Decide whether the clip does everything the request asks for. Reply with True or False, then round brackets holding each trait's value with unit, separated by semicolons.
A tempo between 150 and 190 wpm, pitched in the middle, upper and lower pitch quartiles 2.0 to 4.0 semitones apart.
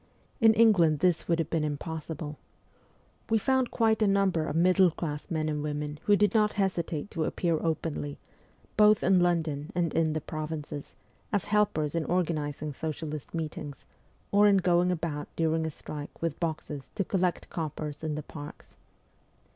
True (165 wpm; 165 Hz; 3.3 semitones)